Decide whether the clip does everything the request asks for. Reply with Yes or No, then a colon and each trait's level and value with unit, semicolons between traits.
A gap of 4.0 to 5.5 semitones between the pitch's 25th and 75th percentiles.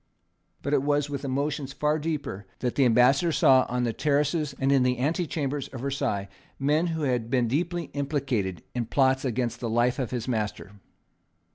No: average, 3.1 semitones